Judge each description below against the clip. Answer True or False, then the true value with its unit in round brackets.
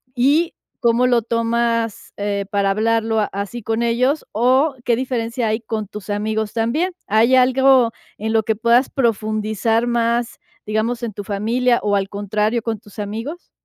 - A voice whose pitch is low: False (230 Hz)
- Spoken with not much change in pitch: True (2.1 semitones)